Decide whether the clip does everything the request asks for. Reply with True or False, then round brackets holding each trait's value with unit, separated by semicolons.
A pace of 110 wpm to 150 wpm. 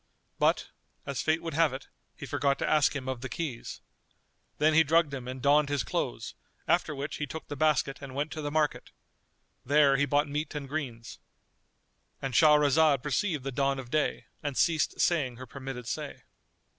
False (180 wpm)